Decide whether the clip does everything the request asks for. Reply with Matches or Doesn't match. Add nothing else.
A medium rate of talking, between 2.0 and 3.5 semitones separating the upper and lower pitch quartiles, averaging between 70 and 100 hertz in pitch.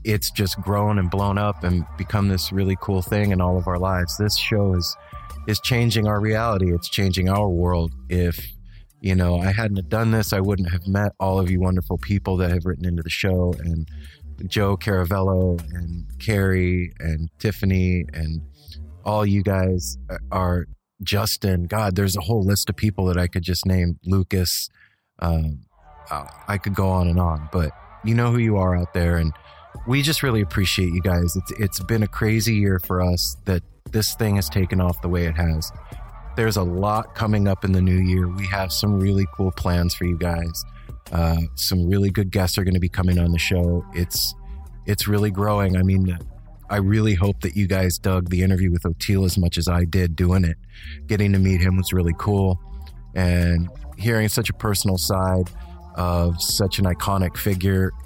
Matches